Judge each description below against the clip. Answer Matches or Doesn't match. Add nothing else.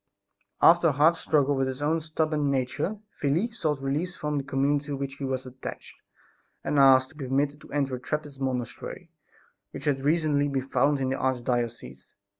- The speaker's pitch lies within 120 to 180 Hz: Matches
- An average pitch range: Doesn't match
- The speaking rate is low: Doesn't match